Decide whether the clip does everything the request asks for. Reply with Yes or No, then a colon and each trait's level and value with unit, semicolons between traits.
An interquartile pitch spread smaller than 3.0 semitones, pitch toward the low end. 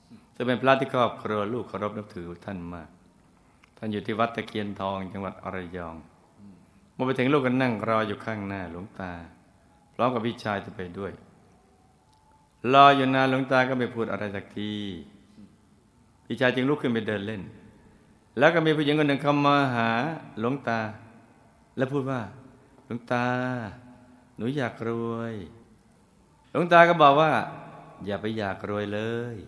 No: average, 4.1 semitones; low, 115 Hz